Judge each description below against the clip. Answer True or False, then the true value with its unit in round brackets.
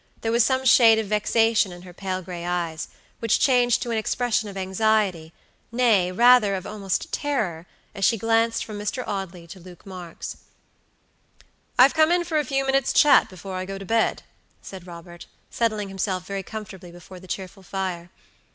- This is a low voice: False (200 Hz)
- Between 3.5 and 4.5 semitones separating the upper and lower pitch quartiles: True (3.9 semitones)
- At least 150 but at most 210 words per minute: True (175 wpm)